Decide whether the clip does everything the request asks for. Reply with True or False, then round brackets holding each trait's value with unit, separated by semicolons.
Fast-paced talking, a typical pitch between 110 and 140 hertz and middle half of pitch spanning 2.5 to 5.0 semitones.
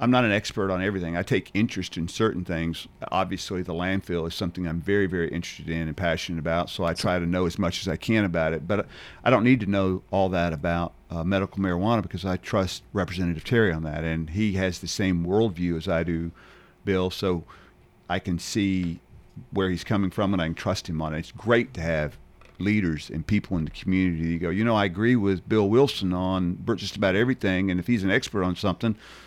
False (230 wpm; 95 Hz; 2.9 semitones)